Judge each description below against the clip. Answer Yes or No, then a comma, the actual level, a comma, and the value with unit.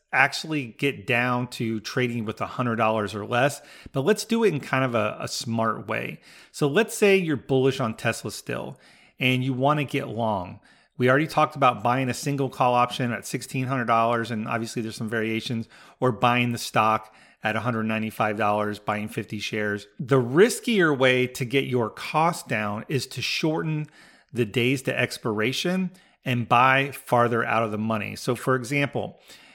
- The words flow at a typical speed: Yes, average, 190 wpm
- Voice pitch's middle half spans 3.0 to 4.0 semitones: Yes, average, 3.6 semitones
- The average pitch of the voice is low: Yes, low, 125 Hz